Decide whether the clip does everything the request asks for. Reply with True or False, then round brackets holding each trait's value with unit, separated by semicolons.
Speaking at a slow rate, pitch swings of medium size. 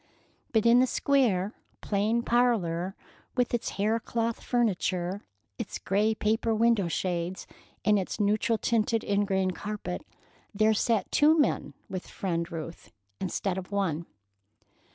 True (130 wpm; 3.7 semitones)